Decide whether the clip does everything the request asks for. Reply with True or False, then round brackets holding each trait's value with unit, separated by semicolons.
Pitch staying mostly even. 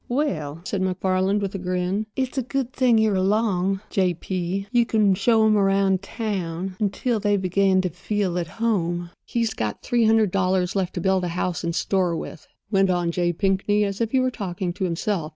False (3.0 semitones)